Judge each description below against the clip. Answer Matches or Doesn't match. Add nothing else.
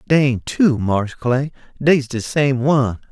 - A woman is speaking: Doesn't match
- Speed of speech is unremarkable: Matches